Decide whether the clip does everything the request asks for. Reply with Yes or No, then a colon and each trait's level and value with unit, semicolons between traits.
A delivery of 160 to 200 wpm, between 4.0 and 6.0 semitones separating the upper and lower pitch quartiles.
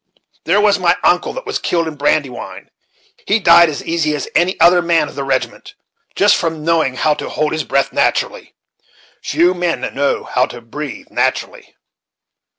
No: average, 170 wpm; average, 3.3 semitones